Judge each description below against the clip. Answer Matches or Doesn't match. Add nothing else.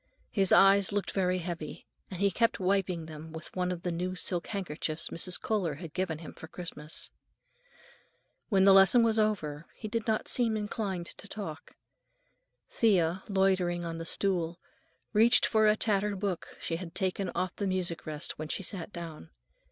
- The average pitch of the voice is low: Doesn't match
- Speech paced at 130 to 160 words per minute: Doesn't match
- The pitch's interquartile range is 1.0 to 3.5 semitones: Matches